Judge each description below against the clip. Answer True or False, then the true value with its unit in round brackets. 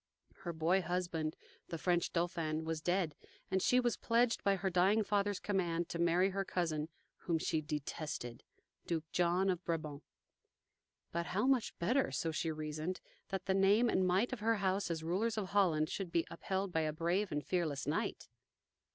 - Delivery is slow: False (175 wpm)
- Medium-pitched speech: True (175 Hz)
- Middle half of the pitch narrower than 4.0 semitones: True (3.2 semitones)